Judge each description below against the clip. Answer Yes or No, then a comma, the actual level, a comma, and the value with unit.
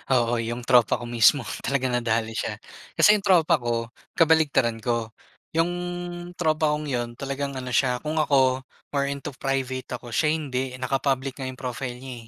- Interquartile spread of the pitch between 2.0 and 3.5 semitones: Yes, average, 3.0 semitones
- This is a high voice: No, low, 130 Hz